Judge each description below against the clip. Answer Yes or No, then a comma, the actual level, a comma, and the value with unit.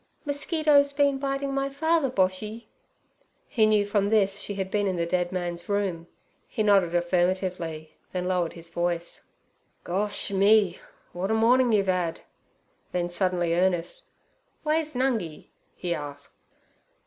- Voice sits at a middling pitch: No, high, 195 Hz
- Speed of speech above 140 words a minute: No, slow, 135 wpm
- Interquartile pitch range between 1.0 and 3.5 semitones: No, average, 4.7 semitones